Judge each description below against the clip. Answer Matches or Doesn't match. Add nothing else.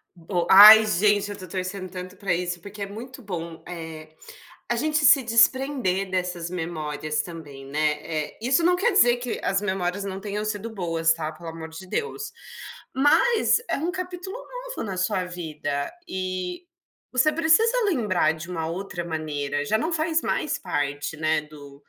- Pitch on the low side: Doesn't match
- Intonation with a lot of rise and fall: Matches